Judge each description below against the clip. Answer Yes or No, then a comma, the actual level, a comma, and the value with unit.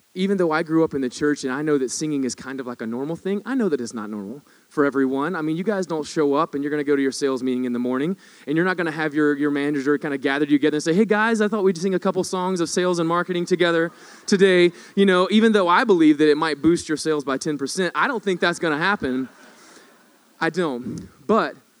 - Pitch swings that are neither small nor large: Yes, average, 4.5 semitones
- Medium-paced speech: No, fast, 280 wpm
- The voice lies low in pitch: No, medium, 160 Hz